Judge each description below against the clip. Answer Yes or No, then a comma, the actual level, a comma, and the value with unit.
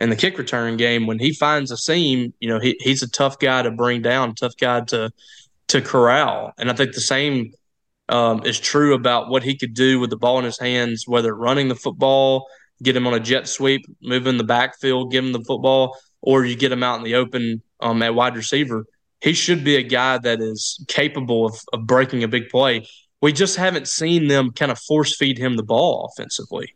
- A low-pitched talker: Yes, low, 125 Hz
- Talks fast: Yes, fast, 225 wpm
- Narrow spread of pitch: Yes, narrow, 2.1 semitones